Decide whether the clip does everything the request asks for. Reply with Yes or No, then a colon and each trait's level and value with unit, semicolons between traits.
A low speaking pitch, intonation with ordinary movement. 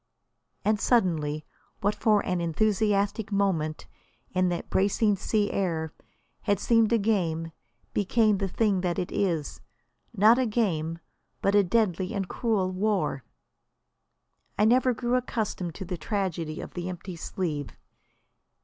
No: high, 195 Hz; average, 3.8 semitones